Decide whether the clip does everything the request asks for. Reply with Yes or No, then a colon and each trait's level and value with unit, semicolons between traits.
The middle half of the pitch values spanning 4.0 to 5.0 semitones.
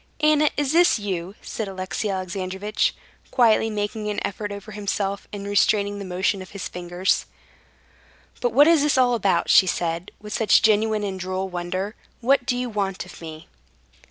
No: average, 3.0 semitones